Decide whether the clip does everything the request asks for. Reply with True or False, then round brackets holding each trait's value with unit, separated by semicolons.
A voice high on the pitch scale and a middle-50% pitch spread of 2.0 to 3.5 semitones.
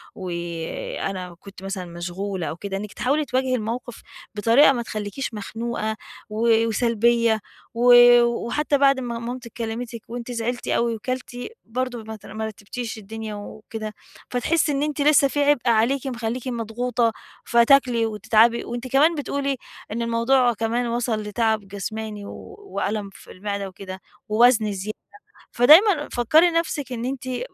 True (235 Hz; 2.9 semitones)